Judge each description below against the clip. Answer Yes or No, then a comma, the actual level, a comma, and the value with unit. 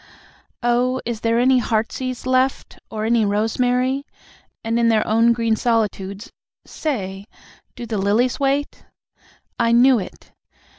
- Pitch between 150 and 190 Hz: No, high, 235 Hz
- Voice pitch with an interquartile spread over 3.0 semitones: No, narrow, 2.5 semitones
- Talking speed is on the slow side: Yes, slow, 130 wpm